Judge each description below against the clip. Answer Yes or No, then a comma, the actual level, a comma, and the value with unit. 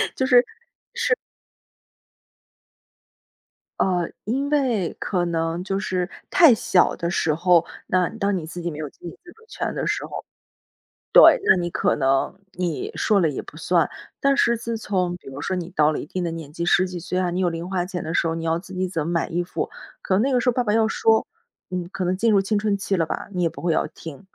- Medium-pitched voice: Yes, medium, 180 Hz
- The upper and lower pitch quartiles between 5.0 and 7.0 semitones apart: No, average, 3.7 semitones